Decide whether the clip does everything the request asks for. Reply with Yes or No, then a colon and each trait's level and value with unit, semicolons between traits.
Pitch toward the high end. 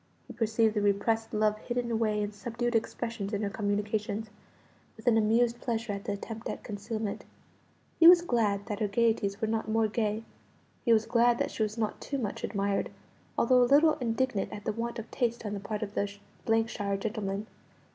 Yes: high, 220 Hz